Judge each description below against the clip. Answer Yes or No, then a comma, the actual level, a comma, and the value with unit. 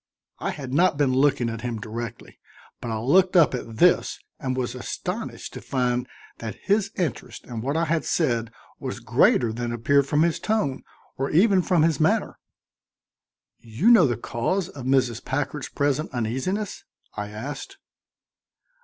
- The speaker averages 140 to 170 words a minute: Yes, average, 160 wpm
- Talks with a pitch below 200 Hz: Yes, low, 135 Hz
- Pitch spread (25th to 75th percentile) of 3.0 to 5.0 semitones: No, wide, 5.6 semitones